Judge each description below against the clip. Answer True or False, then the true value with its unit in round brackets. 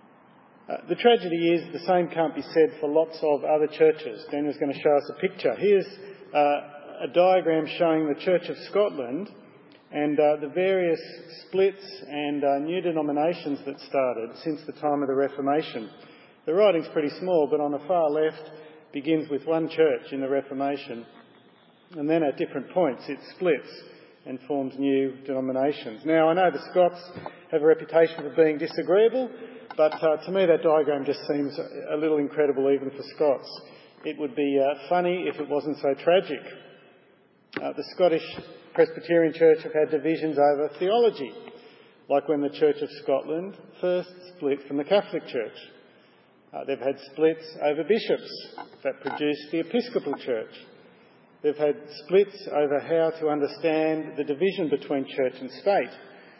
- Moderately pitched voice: True (155 Hz)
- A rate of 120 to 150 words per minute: False (165 wpm)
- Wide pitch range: False (3.4 semitones)